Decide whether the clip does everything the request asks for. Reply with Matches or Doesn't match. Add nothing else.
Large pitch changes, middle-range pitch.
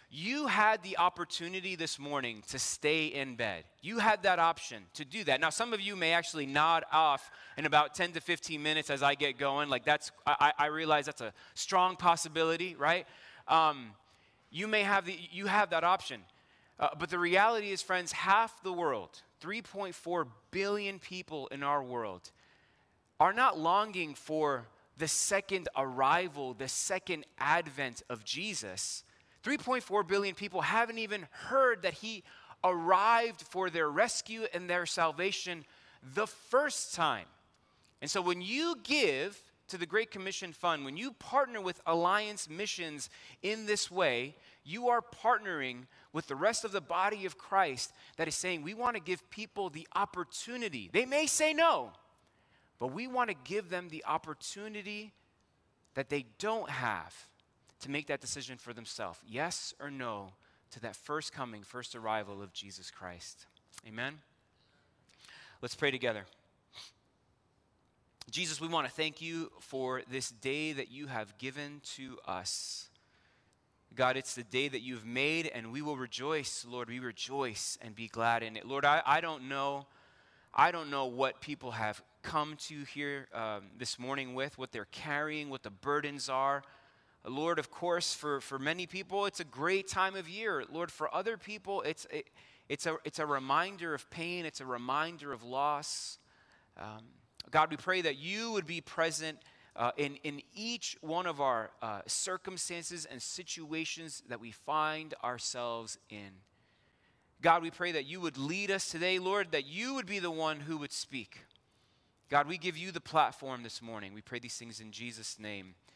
Matches